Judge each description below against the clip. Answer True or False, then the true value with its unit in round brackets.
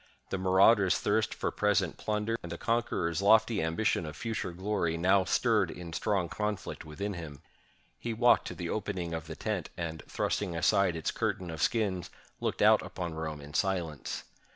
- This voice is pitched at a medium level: False (95 Hz)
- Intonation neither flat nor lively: True (3.9 semitones)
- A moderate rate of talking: True (175 wpm)